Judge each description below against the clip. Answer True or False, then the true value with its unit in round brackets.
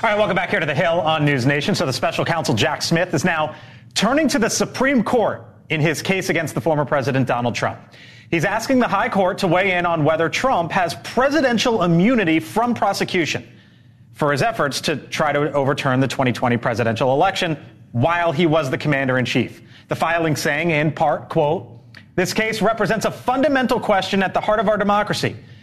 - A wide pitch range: True (7.0 semitones)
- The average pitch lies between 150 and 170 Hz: True (165 Hz)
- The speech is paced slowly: False (200 wpm)